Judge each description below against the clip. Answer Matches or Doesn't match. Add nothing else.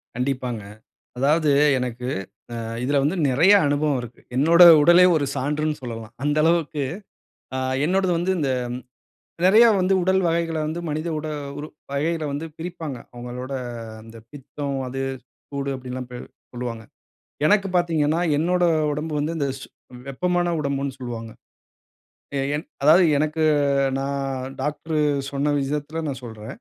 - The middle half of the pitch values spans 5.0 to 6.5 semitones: Doesn't match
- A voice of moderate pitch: Matches